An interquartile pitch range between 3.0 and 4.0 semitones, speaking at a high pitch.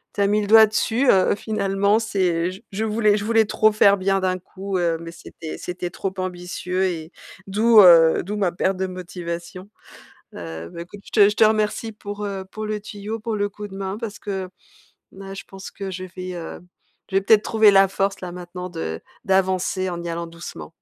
No: narrow, 2.6 semitones; high, 195 Hz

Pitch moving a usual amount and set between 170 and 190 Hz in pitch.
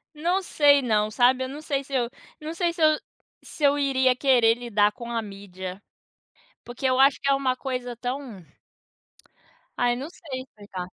No: average, 3.7 semitones; very high, 255 Hz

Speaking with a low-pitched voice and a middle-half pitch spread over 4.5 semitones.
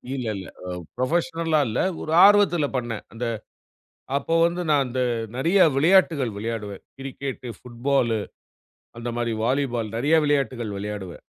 Yes: low, 130 Hz; average, 5.1 semitones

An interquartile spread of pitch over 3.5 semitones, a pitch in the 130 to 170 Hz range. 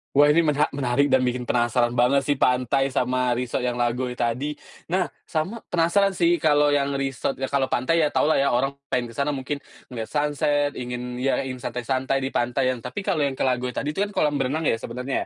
No: average, 2.9 semitones; low, 135 Hz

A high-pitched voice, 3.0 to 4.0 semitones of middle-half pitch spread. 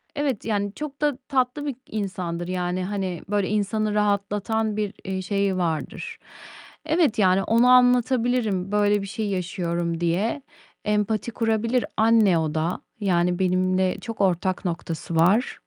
Yes: high, 205 Hz; average, 3.6 semitones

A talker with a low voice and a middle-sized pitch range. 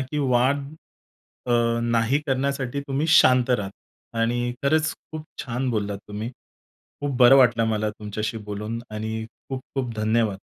Yes: low, 120 Hz; average, 3.6 semitones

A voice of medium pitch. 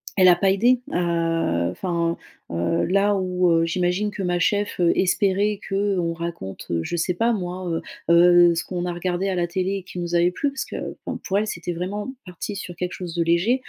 Yes: medium, 180 Hz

